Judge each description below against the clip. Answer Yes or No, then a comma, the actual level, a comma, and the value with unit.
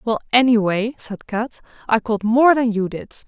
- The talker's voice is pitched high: Yes, high, 225 Hz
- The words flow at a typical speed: Yes, average, 185 wpm